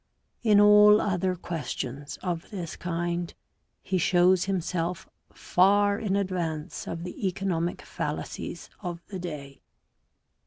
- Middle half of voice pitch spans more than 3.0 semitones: No, narrow, 2.6 semitones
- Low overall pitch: No, medium, 180 Hz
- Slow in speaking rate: Yes, slow, 115 wpm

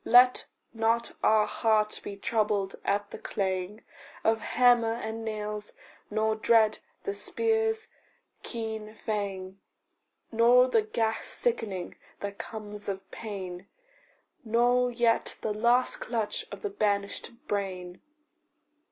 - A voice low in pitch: No, high, 220 Hz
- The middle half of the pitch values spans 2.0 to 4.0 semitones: Yes, narrow, 2.6 semitones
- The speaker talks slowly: Yes, slow, 115 wpm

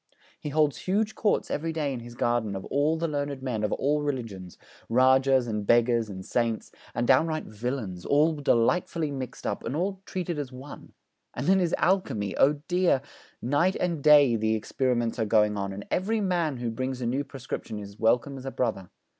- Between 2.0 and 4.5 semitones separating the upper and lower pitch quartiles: No, average, 5.0 semitones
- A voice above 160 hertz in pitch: No, low, 130 Hz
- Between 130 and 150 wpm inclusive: No, average, 190 wpm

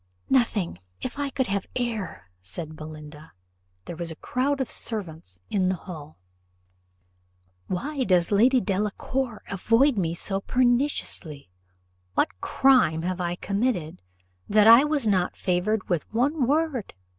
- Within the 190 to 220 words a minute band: No, slow, 135 wpm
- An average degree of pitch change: No, wide, 6.9 semitones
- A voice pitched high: Yes, high, 200 Hz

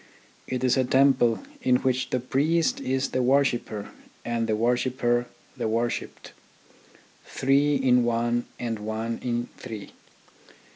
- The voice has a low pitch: Yes, low, 125 Hz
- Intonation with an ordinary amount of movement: No, narrow, 2.0 semitones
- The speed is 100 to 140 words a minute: Yes, slow, 135 wpm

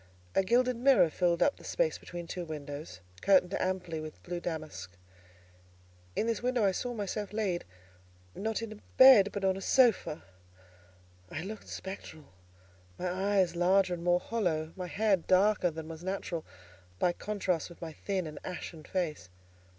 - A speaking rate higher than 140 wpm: Yes, average, 160 wpm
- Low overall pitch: No, medium, 185 Hz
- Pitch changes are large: No, average, 3.7 semitones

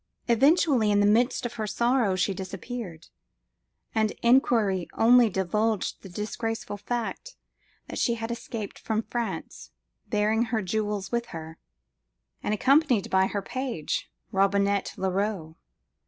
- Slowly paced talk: Yes, slow, 125 wpm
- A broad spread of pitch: No, average, 3.3 semitones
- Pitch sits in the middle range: No, high, 215 Hz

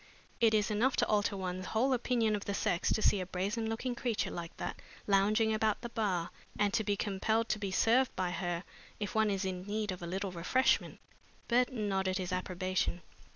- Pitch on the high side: Yes, high, 205 Hz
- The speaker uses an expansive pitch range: No, average, 3.1 semitones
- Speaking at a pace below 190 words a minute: No, average, 200 wpm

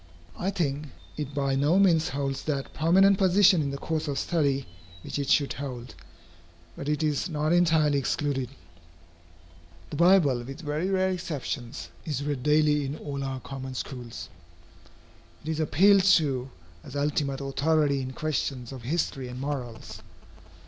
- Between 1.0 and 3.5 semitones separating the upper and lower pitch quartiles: Yes, average, 2.9 semitones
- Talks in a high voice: No, medium, 145 Hz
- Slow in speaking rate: No, average, 150 wpm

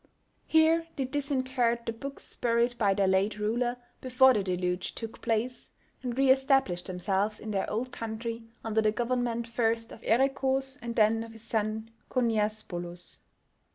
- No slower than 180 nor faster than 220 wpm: No, average, 155 wpm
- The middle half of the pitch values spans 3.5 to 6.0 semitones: No, average, 3.0 semitones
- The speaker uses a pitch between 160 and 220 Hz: No, high, 230 Hz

